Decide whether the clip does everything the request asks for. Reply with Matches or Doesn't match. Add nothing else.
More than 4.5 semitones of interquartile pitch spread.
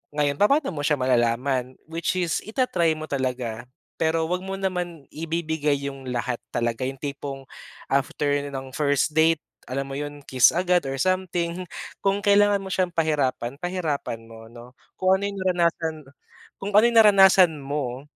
Matches